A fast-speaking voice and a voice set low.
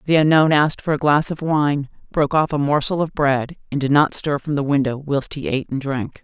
No: fast, 250 wpm; medium, 145 Hz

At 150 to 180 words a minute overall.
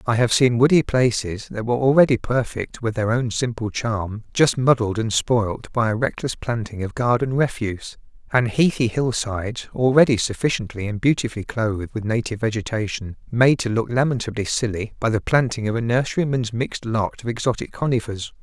Yes: average, 170 wpm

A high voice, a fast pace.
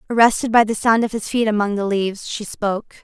Yes: high, 215 Hz; fast, 235 wpm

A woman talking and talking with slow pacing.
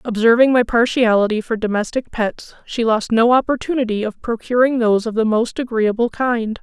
No: female; average, 165 wpm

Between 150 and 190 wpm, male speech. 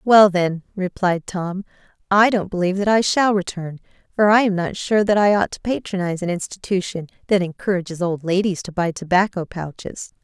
No: average, 180 wpm; female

